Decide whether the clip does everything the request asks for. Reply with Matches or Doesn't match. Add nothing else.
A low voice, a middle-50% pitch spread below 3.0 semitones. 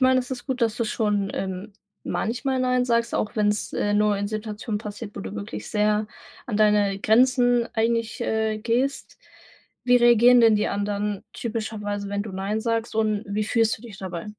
Doesn't match